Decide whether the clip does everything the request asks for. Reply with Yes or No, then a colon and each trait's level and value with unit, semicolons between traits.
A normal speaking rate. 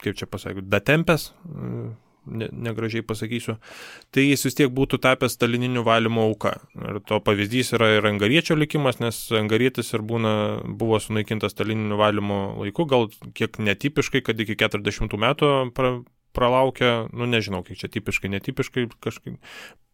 Yes: average, 145 wpm